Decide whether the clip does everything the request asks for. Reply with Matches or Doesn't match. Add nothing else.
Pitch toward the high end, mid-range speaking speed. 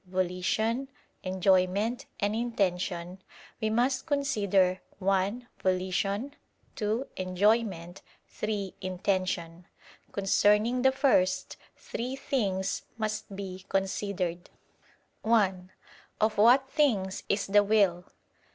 Doesn't match